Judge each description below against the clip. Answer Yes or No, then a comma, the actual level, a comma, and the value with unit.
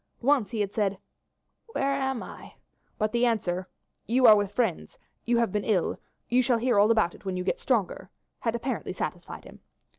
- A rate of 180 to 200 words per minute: Yes, average, 190 wpm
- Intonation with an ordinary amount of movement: Yes, average, 3.3 semitones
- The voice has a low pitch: No, high, 225 Hz